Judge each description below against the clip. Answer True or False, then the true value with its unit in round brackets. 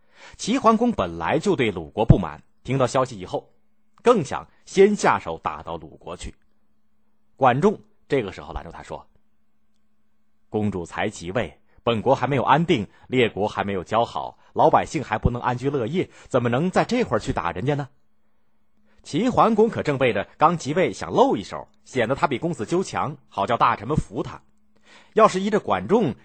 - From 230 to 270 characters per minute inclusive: True (260 characters per minute)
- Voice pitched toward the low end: True (130 Hz)